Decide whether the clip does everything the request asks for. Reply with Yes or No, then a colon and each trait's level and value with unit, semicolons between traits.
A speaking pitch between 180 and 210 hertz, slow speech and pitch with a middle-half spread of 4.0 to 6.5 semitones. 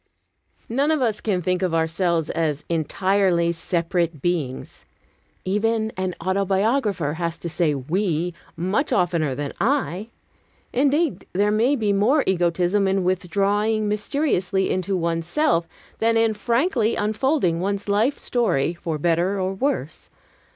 Yes: high, 190 Hz; slow, 130 wpm; average, 4.4 semitones